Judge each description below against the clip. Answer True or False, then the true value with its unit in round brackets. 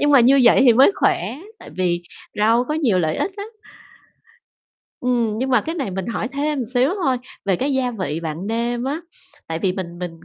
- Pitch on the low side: False (240 Hz)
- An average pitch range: False (6.5 semitones)